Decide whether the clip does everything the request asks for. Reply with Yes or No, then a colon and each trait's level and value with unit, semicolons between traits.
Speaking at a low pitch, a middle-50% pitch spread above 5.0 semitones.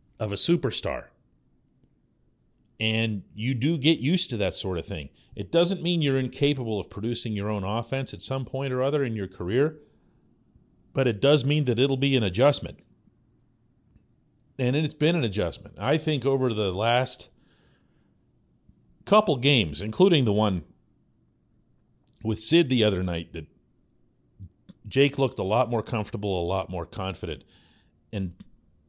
Yes: low, 115 Hz; wide, 5.5 semitones